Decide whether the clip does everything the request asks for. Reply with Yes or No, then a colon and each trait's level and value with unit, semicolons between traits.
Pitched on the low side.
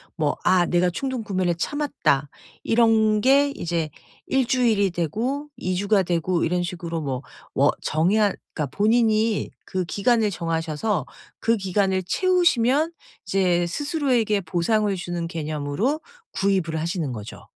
No: high, 190 Hz